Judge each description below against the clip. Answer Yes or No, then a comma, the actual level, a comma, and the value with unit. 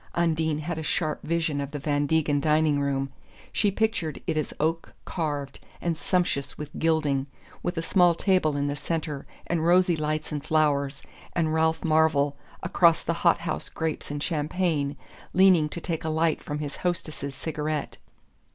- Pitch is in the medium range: Yes, medium, 155 Hz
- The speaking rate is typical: Yes, average, 170 wpm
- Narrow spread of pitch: Yes, narrow, 2.3 semitones